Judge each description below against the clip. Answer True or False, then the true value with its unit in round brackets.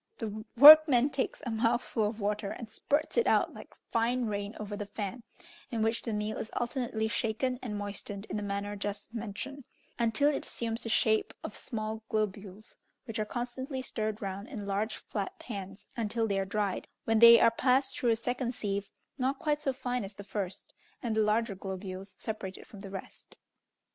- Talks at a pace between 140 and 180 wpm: False (190 wpm)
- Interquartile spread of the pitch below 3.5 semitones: True (2.8 semitones)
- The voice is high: True (220 Hz)